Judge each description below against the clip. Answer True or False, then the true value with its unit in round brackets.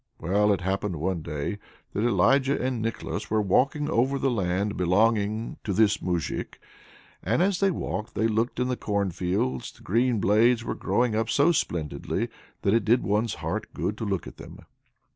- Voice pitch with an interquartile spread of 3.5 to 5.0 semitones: True (3.9 semitones)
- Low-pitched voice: True (110 Hz)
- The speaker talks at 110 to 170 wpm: False (180 wpm)